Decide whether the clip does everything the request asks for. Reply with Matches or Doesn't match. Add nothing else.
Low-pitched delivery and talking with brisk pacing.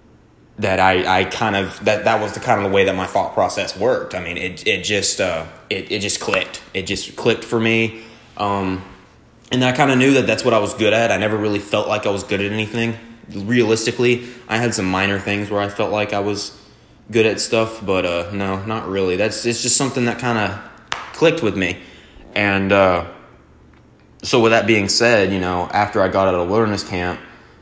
Matches